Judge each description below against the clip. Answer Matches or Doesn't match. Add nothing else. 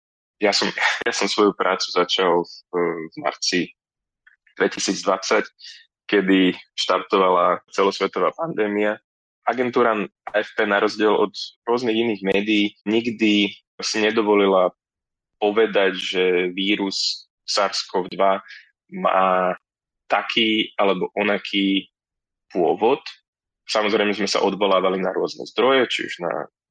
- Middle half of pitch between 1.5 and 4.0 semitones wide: Matches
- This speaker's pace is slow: Matches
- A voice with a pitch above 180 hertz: Doesn't match